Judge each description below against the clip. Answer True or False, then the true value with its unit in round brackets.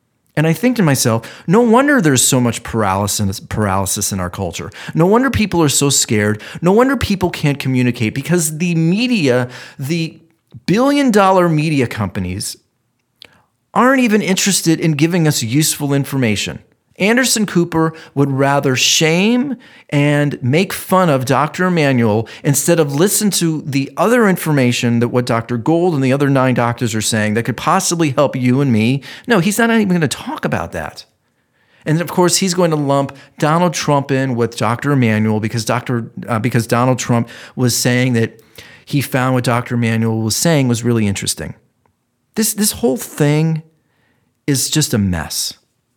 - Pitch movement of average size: False (6.1 semitones)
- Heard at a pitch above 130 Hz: True (140 Hz)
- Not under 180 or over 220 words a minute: False (165 wpm)